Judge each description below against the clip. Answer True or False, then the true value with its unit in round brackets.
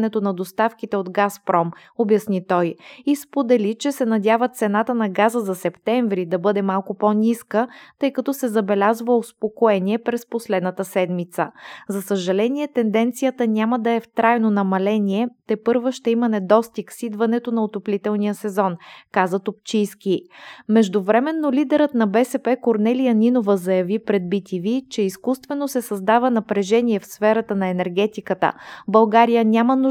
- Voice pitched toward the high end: True (220 Hz)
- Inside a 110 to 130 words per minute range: False (140 wpm)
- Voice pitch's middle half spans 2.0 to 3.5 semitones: True (2.9 semitones)